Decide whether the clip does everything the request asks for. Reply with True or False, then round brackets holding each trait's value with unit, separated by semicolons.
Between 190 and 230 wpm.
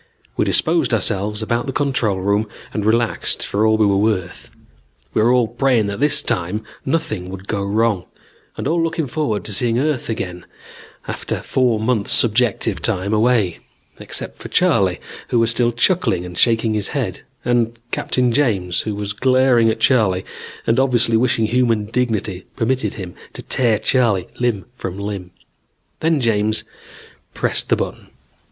False (160 wpm)